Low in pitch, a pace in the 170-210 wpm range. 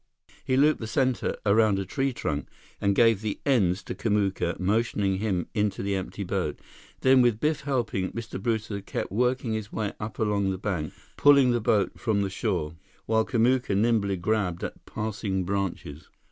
Yes: low, 105 Hz; average, 175 wpm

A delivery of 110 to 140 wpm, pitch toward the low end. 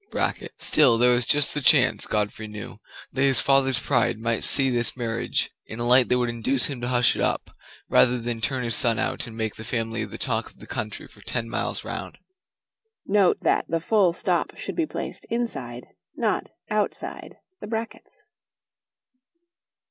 No: average, 180 wpm; low, 125 Hz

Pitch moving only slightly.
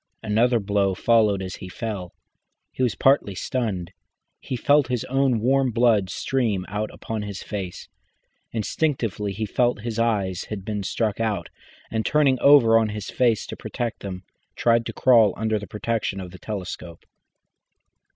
No: average, 3.3 semitones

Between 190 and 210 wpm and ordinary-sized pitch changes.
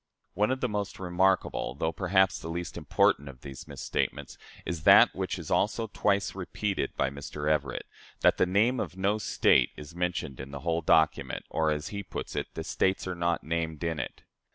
Yes: average, 195 wpm; average, 4.0 semitones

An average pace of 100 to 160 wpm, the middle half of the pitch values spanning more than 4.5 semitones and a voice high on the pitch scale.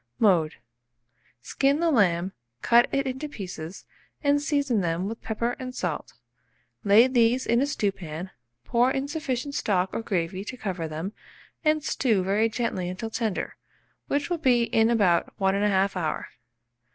Yes: average, 150 wpm; wide, 5.5 semitones; high, 225 Hz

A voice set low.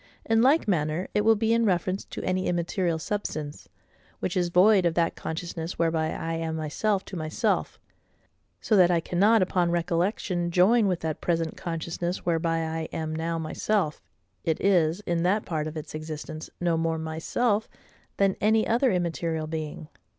No: medium, 170 Hz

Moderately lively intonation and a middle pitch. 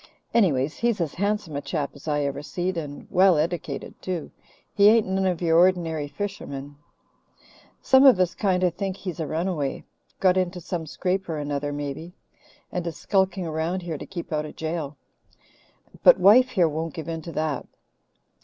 Yes: average, 3.7 semitones; medium, 170 Hz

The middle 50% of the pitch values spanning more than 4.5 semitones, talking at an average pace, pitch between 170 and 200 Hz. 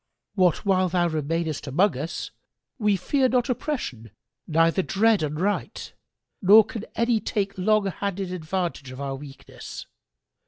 No: average, 5.0 semitones; slow, 130 wpm; medium, 185 Hz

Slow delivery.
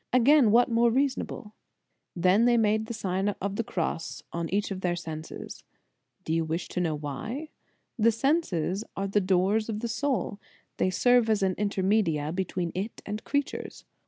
No: average, 165 wpm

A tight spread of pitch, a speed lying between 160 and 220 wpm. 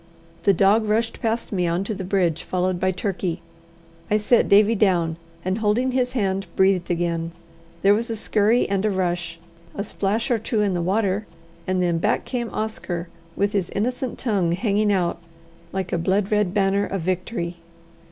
No: average, 3.1 semitones; average, 180 wpm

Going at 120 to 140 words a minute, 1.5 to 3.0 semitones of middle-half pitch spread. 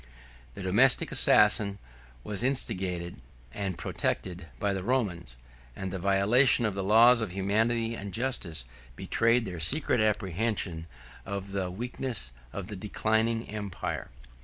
No: slow, 135 wpm; average, 3.6 semitones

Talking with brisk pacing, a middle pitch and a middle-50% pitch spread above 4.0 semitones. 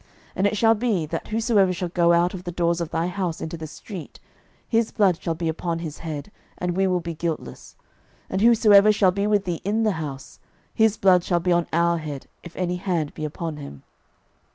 No: fast, 220 wpm; medium, 175 Hz; average, 3.3 semitones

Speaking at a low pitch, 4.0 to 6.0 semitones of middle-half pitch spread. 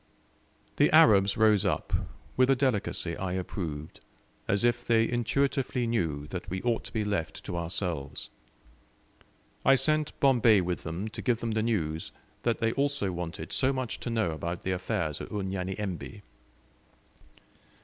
Yes: low, 105 Hz; average, 5.2 semitones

